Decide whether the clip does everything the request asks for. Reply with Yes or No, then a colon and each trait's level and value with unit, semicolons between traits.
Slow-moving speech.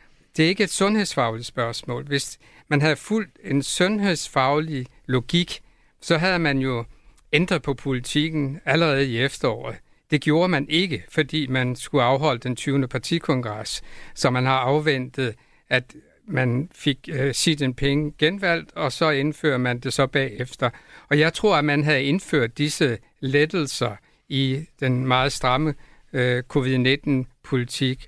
Yes: slow, 140 wpm